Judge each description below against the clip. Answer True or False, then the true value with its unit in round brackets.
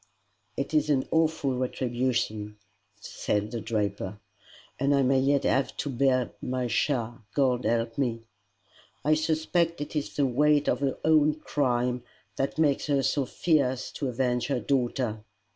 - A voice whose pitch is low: True (130 Hz)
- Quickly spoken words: False (150 wpm)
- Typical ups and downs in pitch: True (3.2 semitones)